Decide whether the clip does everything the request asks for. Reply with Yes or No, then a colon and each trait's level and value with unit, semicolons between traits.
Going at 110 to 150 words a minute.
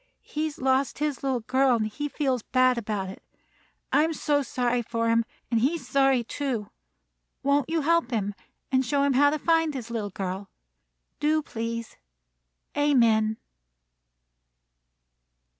Yes: average, 140 wpm